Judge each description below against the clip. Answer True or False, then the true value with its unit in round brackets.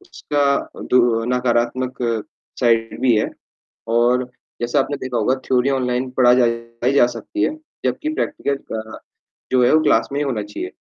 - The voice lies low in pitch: True (125 Hz)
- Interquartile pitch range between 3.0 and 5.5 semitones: False (2.4 semitones)